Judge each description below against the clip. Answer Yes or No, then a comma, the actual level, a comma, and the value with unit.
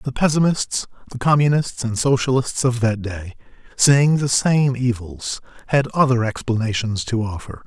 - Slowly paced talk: Yes, slow, 125 wpm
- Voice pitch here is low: Yes, low, 125 Hz